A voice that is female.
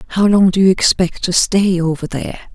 Yes: female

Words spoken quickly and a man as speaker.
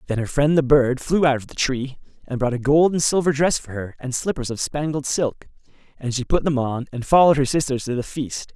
Yes: fast, 255 wpm; male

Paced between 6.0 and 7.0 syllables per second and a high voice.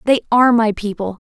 Yes: 6.3 syllables/s; high, 225 Hz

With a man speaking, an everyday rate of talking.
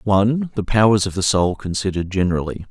Yes: male; average, 175 wpm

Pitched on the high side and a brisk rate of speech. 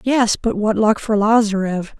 No: high, 215 Hz; average, 180 wpm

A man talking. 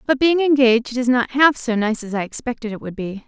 No: female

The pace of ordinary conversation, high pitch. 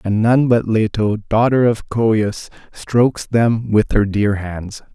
No: average, 160 wpm; low, 110 Hz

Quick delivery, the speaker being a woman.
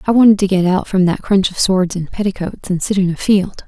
Yes: fast, 275 wpm; female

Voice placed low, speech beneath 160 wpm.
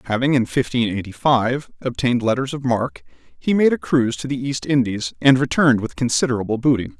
No: low, 125 Hz; average, 190 wpm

